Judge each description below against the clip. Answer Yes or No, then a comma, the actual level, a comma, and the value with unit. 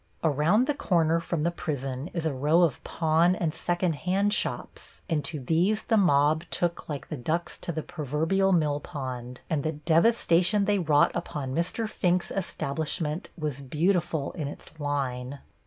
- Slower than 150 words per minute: No, average, 165 wpm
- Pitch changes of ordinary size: Yes, average, 3.4 semitones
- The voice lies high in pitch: No, medium, 160 Hz